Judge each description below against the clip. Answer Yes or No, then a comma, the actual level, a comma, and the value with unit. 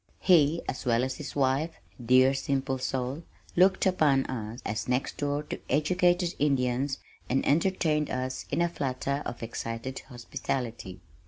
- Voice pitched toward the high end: No, low, 135 Hz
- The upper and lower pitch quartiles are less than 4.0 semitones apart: Yes, average, 3.2 semitones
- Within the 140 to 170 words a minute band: Yes, average, 145 wpm